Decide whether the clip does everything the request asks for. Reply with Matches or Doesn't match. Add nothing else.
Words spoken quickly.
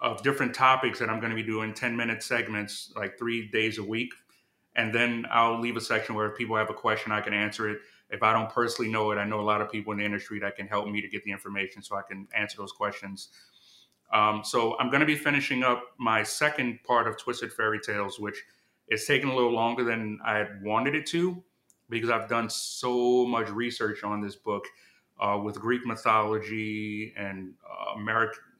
Matches